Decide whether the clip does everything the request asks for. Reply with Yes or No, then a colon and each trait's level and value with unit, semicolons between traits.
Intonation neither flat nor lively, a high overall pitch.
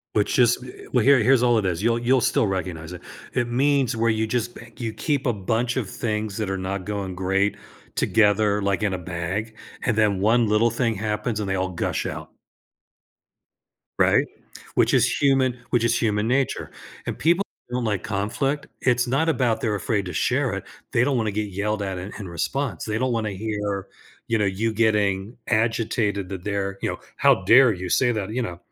No: average, 3.4 semitones; low, 110 Hz